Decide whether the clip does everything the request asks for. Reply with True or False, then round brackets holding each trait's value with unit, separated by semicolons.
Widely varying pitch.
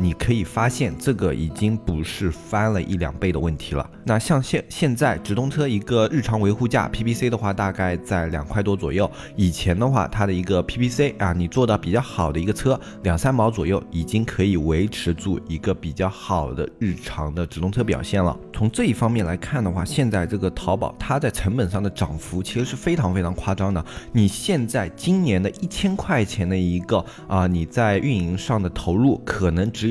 False (4.8 semitones)